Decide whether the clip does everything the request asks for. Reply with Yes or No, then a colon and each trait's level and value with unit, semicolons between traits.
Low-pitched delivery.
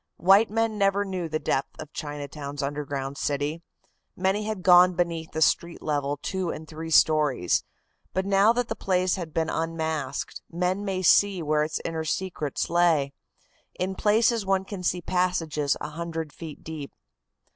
No: medium, 165 Hz